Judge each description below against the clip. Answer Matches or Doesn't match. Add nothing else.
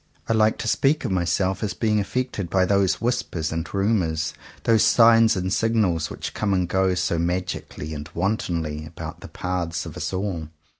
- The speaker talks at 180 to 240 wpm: Matches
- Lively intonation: Doesn't match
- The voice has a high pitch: Doesn't match